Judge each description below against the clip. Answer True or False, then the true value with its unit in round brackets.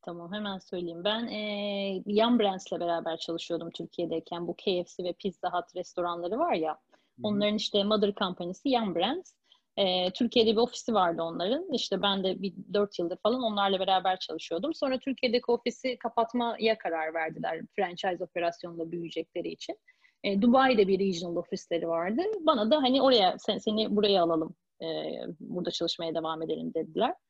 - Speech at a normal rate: False (155 wpm)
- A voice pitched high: True (195 Hz)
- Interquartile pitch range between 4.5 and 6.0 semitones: True (5.1 semitones)